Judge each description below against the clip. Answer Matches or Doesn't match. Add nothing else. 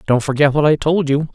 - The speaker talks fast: Matches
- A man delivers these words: Matches